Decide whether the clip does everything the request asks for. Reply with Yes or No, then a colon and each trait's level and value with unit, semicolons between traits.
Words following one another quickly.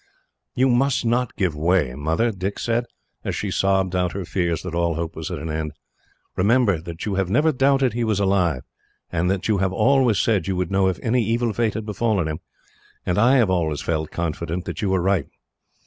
Yes: fast, 210 wpm